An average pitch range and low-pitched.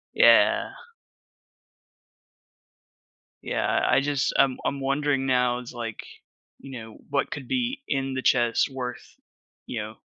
No: narrow, 2.2 semitones; low, 130 Hz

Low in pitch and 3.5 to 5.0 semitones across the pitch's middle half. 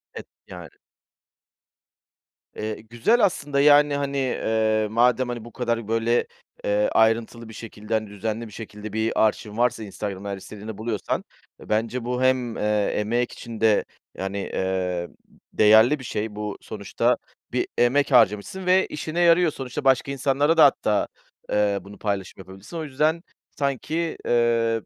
Yes: low, 115 Hz; average, 3.9 semitones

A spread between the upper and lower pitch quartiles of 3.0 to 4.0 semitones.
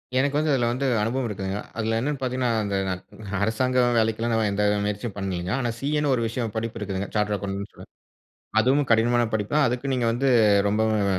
Yes: average, 3.6 semitones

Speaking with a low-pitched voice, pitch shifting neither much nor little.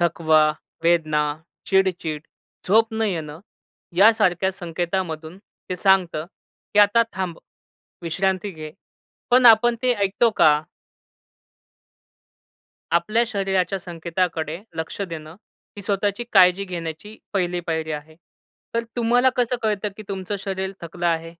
No: medium, 185 Hz; average, 3.7 semitones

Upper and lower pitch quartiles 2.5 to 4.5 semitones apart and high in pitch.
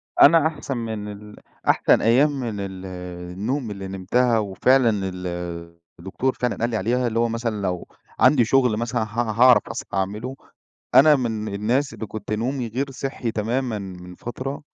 No: average, 3.7 semitones; low, 115 Hz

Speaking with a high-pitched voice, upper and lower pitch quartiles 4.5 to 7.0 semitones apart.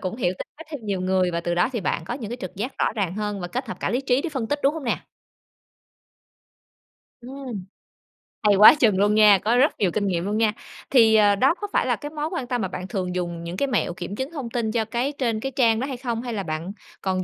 Yes: high, 220 Hz; average, 5.1 semitones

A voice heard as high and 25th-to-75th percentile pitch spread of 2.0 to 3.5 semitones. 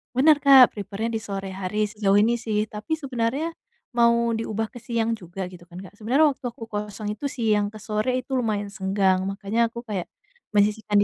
Yes: high, 220 Hz; narrow, 2.6 semitones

